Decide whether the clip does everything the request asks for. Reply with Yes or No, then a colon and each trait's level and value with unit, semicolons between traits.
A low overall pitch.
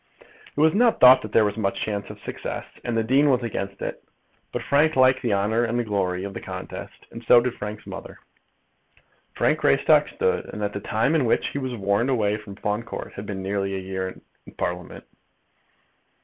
Yes: low, 110 Hz